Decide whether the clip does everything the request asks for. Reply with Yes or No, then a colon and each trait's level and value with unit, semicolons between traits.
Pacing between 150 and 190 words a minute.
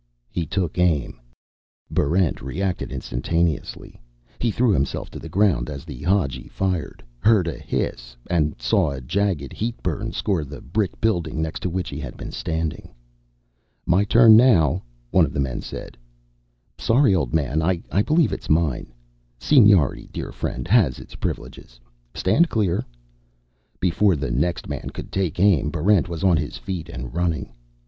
Yes: average, 155 wpm